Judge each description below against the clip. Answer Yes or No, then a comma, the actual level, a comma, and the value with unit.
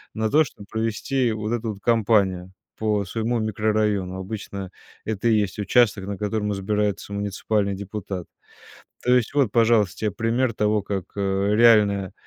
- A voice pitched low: Yes, low, 105 Hz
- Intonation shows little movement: Yes, narrow, 2.0 semitones